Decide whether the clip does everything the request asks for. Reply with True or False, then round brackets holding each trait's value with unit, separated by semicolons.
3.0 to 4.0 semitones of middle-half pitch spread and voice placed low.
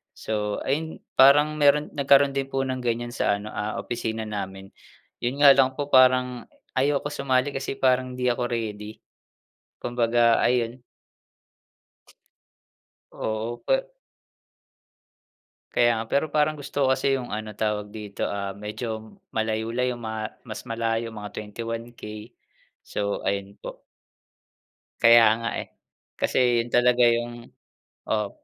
True (3.3 semitones; 120 Hz)